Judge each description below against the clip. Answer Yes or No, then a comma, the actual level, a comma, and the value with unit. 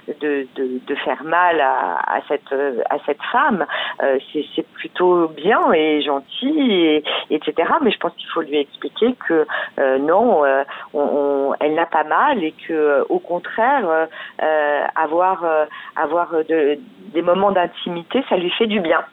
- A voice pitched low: No, medium, 160 Hz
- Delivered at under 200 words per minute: Yes, average, 175 wpm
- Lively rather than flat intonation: No, average, 3.4 semitones